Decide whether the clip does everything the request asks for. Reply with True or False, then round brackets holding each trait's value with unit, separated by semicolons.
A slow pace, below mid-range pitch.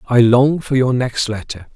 False (205 wpm; 125 Hz)